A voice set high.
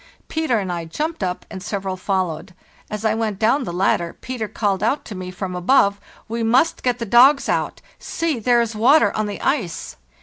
Yes: high, 215 Hz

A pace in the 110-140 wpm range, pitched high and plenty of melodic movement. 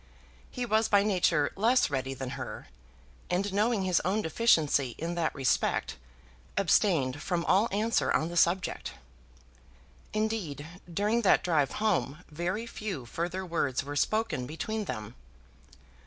No: slow, 135 wpm; medium, 180 Hz; wide, 6.4 semitones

